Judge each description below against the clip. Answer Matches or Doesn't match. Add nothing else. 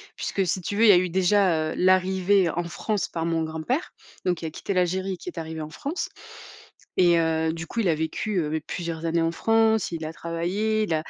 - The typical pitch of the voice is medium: Matches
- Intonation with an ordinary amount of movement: Matches